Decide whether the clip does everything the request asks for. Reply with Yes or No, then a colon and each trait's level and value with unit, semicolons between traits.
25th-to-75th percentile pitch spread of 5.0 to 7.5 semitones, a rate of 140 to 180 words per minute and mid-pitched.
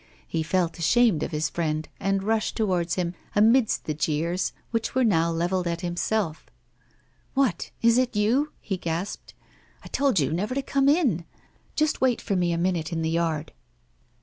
Yes: wide, 5.6 semitones; average, 175 wpm; medium, 180 Hz